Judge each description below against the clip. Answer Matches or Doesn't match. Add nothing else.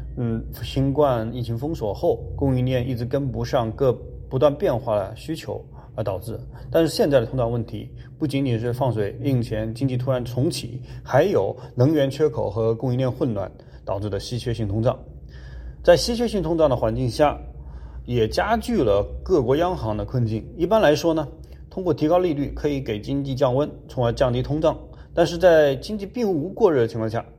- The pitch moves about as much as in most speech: Matches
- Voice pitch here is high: Doesn't match